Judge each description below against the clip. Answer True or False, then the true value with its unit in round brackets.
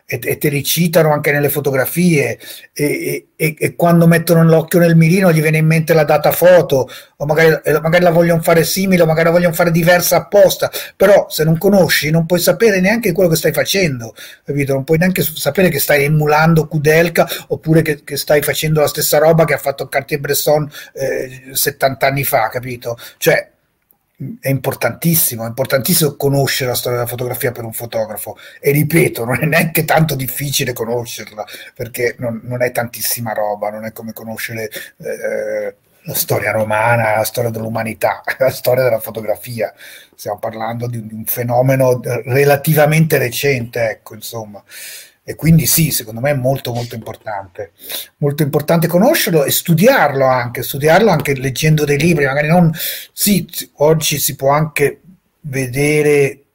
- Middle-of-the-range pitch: True (145 Hz)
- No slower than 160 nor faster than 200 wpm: True (165 wpm)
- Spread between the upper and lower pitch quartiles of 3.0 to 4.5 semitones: False (4.9 semitones)